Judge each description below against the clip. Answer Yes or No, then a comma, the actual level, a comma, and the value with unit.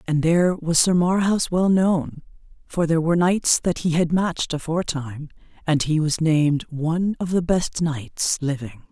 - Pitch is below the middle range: No, medium, 165 Hz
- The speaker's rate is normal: Yes, average, 175 wpm